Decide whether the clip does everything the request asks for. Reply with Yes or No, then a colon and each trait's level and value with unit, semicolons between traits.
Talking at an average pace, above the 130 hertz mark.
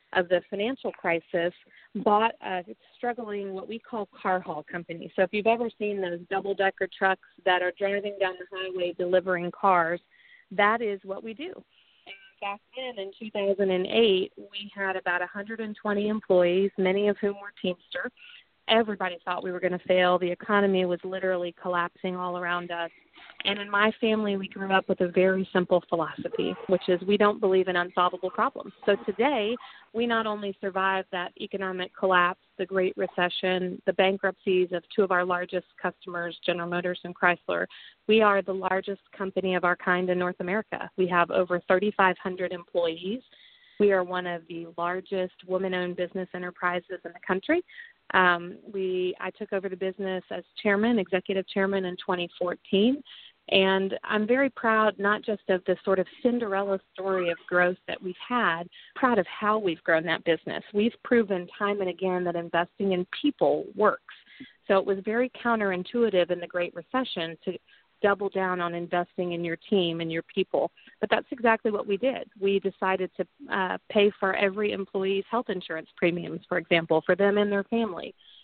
Yes: average, 175 wpm; high, 190 Hz